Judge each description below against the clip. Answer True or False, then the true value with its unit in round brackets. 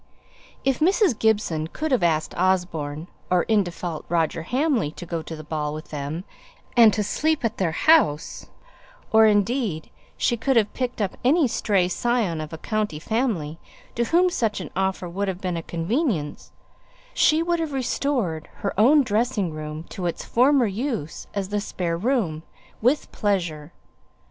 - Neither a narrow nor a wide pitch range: False (6.9 semitones)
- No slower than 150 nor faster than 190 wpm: True (170 wpm)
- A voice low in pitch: False (200 Hz)